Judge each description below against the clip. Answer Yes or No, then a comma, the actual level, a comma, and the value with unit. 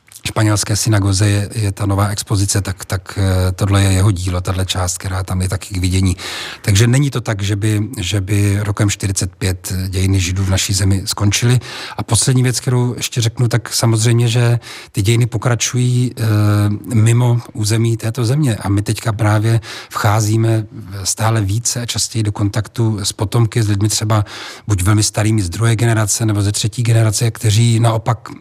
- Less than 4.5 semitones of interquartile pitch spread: Yes, narrow, 2.5 semitones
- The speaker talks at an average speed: No, fast, 175 wpm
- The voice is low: Yes, low, 110 Hz